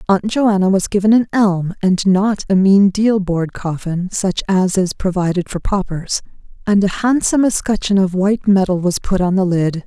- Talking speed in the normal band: Yes, average, 190 wpm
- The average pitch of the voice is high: Yes, high, 195 Hz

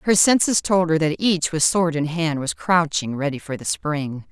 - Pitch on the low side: No, medium, 165 Hz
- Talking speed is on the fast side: Yes, fast, 225 wpm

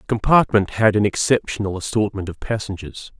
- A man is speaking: Yes, male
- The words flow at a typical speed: Yes, average, 150 wpm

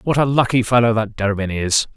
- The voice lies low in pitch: Yes, low, 115 Hz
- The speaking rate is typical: No, fast, 215 wpm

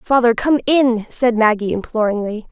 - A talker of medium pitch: No, high, 230 Hz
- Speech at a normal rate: Yes, average, 145 wpm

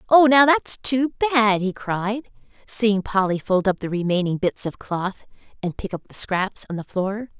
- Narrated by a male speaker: No, female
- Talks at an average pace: Yes, average, 195 wpm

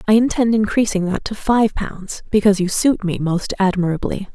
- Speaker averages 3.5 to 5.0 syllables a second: No, 5.2 syllables/s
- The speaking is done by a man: No, female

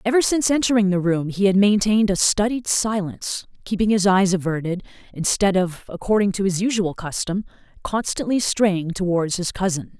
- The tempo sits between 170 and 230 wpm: No, average, 160 wpm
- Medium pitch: No, high, 195 Hz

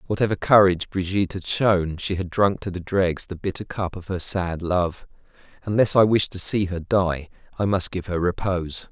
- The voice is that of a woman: No, male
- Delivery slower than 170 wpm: No, average, 200 wpm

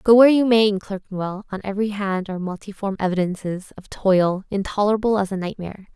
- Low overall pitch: No, high, 200 Hz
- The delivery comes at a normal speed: Yes, average, 180 wpm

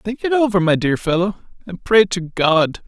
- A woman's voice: No, male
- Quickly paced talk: Yes, fast, 210 wpm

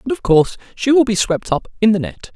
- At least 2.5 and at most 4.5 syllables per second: No, 6.0 syllables/s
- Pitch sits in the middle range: No, high, 205 Hz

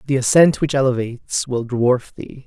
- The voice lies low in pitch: Yes, low, 130 Hz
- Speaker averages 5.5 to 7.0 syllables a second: No, 4.8 syllables/s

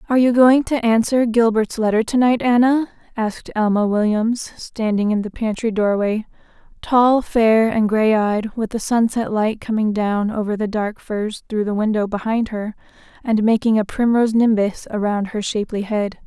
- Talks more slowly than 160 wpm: No, average, 170 wpm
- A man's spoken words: No, female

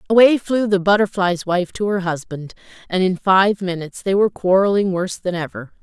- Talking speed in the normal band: Yes, average, 185 wpm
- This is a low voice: No, high, 190 Hz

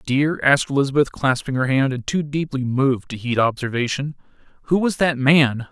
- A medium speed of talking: Yes, average, 180 wpm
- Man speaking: Yes, male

